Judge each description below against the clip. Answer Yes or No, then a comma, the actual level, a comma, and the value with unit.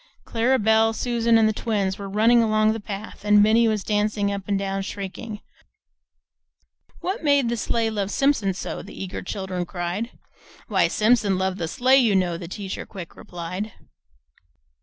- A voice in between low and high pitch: No, high, 210 Hz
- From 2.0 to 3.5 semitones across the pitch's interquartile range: Yes, average, 2.8 semitones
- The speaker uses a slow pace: No, average, 165 wpm